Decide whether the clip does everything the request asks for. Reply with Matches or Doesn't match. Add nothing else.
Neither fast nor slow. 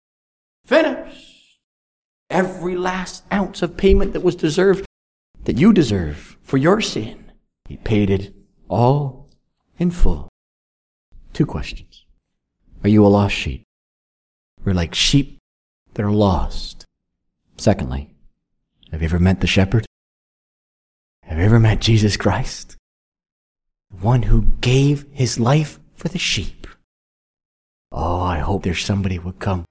Doesn't match